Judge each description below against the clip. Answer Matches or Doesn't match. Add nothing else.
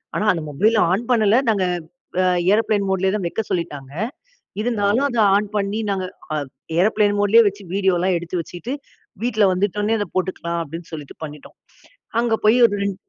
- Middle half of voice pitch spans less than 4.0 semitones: Matches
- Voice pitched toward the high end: Matches